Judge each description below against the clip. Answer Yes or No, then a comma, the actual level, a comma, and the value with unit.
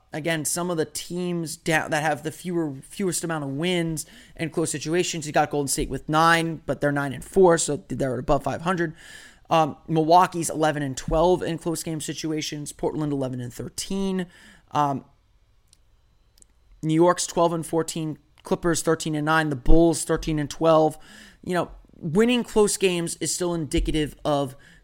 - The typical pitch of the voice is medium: Yes, medium, 160 Hz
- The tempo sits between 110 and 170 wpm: Yes, average, 165 wpm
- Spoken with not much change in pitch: Yes, narrow, 2.3 semitones